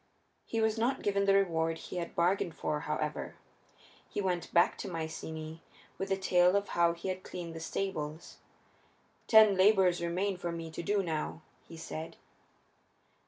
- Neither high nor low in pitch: Yes, medium, 175 Hz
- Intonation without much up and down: No, average, 3.2 semitones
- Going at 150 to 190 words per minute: Yes, average, 165 wpm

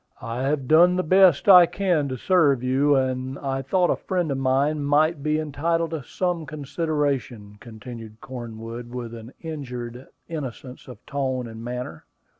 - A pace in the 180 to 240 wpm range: No, average, 160 wpm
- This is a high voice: No, low, 135 Hz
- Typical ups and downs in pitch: Yes, average, 4.1 semitones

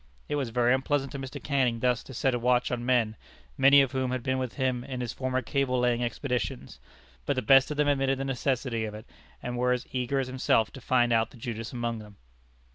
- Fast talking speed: Yes, fast, 235 wpm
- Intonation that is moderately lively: No, narrow, 1.9 semitones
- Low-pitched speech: Yes, low, 125 Hz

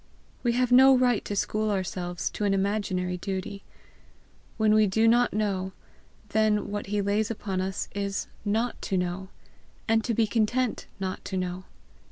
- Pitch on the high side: Yes, high, 205 Hz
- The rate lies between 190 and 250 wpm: No, average, 165 wpm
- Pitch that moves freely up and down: No, average, 2.7 semitones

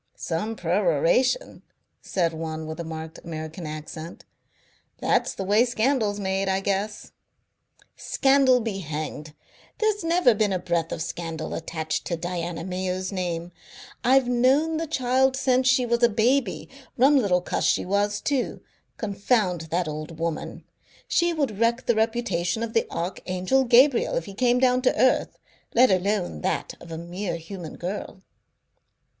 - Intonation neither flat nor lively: No, wide, 6.6 semitones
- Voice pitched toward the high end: Yes, high, 195 Hz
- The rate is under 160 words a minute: Yes, average, 150 wpm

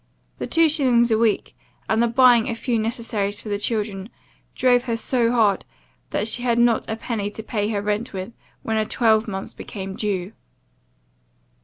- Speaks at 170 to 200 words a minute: Yes, average, 175 wpm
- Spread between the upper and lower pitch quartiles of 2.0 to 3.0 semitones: Yes, narrow, 2.4 semitones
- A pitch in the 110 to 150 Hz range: No, high, 225 Hz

